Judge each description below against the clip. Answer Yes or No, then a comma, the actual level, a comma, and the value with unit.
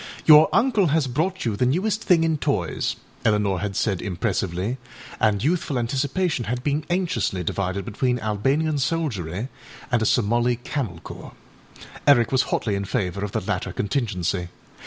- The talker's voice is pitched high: No, low, 120 Hz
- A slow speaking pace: No, average, 155 wpm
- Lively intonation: Yes, wide, 7.0 semitones